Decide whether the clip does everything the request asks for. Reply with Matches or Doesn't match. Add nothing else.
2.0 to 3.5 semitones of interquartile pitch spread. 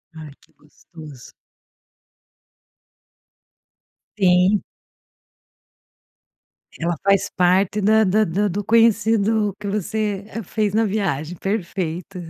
Matches